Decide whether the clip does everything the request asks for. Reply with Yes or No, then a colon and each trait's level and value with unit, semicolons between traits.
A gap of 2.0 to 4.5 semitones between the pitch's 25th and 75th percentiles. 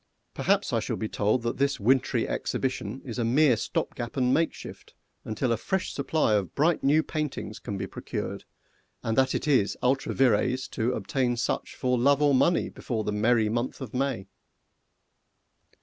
Yes: average, 3.7 semitones